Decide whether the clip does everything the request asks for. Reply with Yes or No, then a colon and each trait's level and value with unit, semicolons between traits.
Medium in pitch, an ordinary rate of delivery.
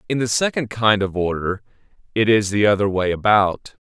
No: low, 105 Hz; average, 185 wpm